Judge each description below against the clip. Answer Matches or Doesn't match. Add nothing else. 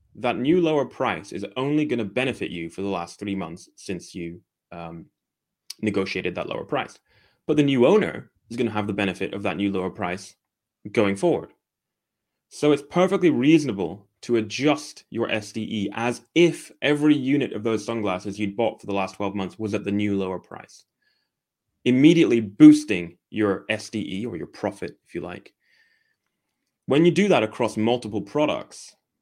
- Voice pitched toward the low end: Matches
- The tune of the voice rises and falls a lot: Matches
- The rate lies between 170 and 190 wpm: Matches